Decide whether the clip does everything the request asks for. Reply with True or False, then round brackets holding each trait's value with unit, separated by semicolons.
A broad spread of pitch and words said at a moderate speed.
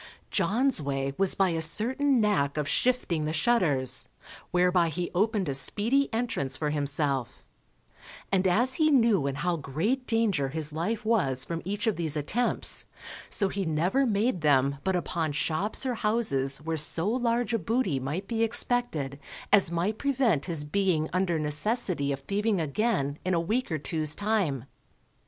True (6.9 semitones; 165 wpm)